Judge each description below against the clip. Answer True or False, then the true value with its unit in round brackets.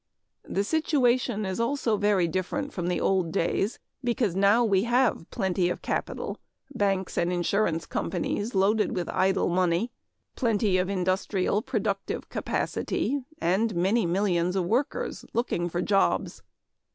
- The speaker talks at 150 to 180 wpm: False (135 wpm)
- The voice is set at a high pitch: True (195 Hz)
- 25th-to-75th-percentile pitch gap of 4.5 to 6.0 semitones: False (4.1 semitones)